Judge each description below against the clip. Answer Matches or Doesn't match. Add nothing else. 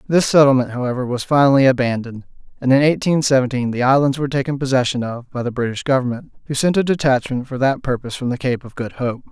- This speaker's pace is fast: Matches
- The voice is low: Matches